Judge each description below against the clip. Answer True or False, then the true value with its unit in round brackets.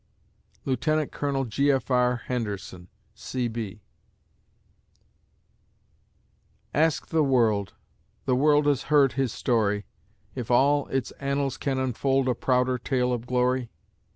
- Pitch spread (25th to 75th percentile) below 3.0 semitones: True (2.5 semitones)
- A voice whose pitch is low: True (130 Hz)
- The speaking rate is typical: False (115 wpm)